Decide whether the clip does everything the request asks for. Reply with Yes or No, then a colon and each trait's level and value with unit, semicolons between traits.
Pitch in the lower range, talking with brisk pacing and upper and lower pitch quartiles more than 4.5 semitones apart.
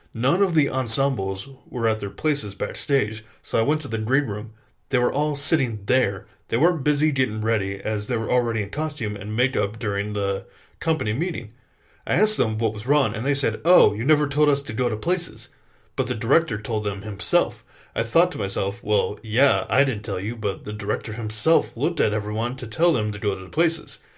Yes: low, 115 Hz; fast, 215 wpm; average, 5.1 semitones